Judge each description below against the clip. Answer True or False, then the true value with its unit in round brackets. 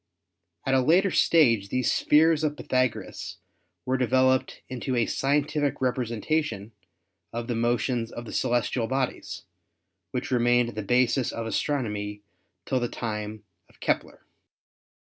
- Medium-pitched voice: False (125 Hz)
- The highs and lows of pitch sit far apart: False (2.7 semitones)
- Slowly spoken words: True (130 wpm)